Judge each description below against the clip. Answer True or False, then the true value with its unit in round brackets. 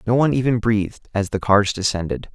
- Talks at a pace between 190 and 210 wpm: True (205 wpm)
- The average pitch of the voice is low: True (110 Hz)